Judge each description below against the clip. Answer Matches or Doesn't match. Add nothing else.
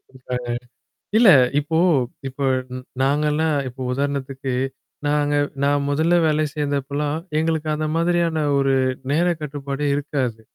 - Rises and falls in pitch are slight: Matches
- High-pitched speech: Doesn't match